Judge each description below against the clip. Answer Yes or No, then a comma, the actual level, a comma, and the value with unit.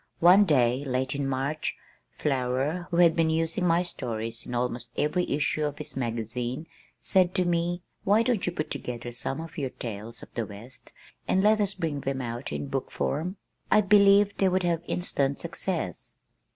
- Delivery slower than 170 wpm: No, average, 180 wpm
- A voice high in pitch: No, medium, 150 Hz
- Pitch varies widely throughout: Yes, wide, 6.0 semitones